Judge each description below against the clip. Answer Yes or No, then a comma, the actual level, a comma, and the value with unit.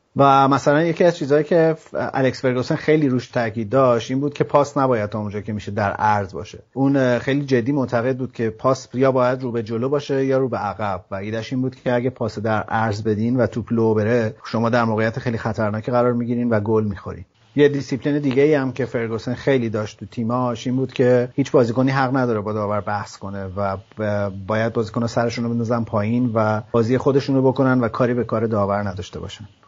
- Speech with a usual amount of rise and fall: Yes, average, 3.5 semitones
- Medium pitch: No, low, 120 Hz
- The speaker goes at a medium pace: No, fast, 210 wpm